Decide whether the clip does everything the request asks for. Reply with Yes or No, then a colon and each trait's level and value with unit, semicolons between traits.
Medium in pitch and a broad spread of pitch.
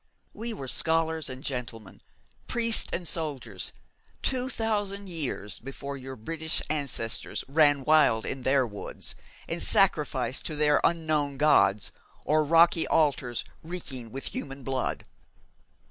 No: medium, 145 Hz; average, 3.8 semitones